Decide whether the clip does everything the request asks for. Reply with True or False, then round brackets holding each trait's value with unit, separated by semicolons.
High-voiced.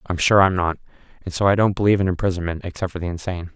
False (90 Hz)